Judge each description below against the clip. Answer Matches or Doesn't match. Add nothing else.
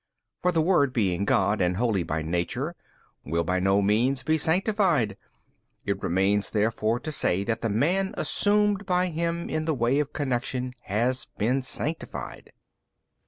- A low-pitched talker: Matches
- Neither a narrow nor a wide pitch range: Doesn't match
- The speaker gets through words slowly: Doesn't match